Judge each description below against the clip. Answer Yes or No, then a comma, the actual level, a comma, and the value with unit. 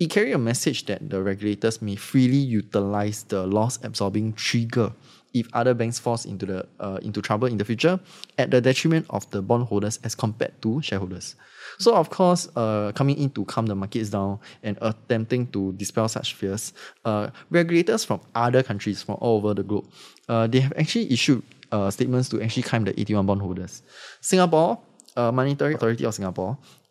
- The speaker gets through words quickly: No, average, 180 wpm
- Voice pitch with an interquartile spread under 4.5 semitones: Yes, average, 4.1 semitones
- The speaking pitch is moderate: No, low, 115 Hz